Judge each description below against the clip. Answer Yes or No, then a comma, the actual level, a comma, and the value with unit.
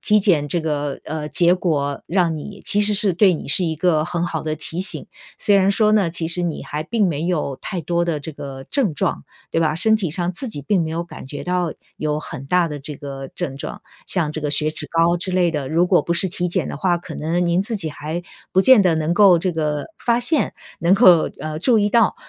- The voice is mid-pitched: Yes, medium, 170 Hz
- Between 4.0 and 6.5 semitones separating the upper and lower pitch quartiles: No, average, 3.4 semitones